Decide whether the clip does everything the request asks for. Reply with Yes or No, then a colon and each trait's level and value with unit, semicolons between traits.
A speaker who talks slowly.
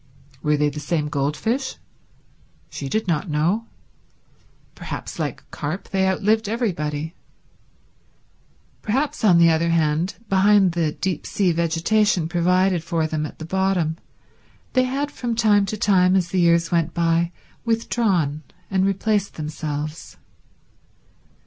Yes: slow, 130 wpm